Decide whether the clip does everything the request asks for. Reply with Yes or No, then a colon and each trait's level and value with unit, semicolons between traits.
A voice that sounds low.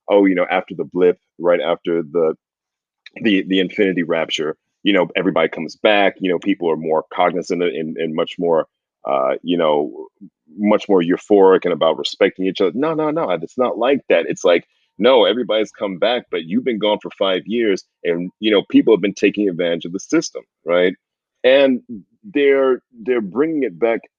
Yes: low, 100 Hz